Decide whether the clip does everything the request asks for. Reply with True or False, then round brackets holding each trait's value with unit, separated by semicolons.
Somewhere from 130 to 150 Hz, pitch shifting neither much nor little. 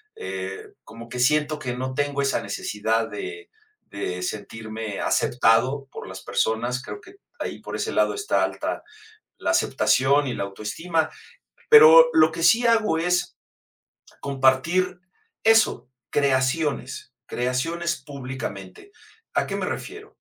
False (135 Hz; 7.1 semitones)